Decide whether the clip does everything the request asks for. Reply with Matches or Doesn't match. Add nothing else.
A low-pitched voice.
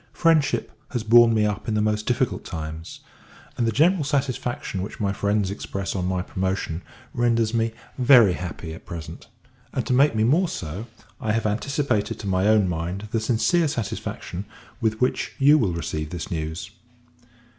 Matches